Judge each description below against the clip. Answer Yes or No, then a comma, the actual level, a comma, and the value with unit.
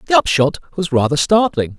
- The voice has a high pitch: No, medium, 165 Hz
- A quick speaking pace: No, average, 170 wpm